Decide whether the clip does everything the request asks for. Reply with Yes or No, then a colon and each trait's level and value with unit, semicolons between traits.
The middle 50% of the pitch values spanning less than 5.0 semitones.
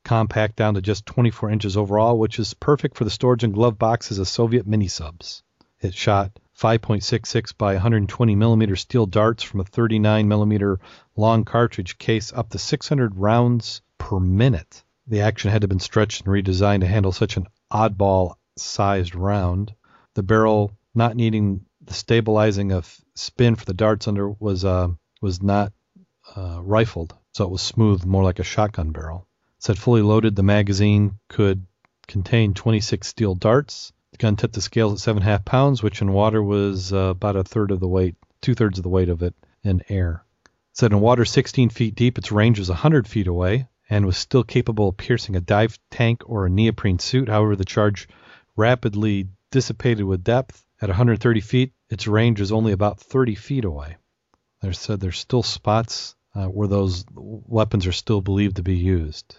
Yes: average, 2.9 semitones